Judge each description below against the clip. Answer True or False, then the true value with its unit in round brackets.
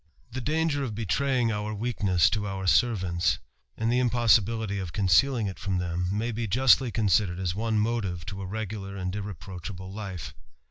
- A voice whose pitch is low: True (105 Hz)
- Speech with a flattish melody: False (3.7 semitones)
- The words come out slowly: False (175 wpm)